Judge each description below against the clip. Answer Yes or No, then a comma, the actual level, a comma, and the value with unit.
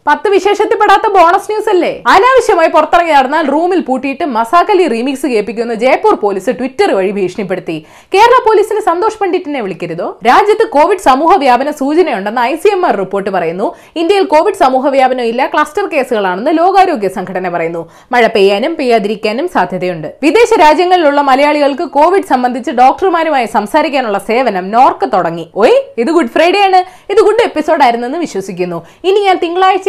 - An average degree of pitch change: No, wide, 8.6 semitones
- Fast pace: Yes, fast, 145 wpm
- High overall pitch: Yes, very high, 300 Hz